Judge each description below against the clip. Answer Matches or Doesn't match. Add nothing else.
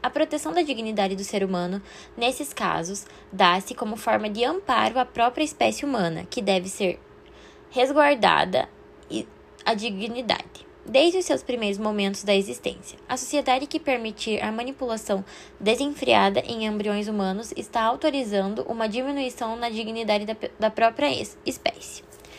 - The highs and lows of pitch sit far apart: Doesn't match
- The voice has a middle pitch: Doesn't match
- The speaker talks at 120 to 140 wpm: Matches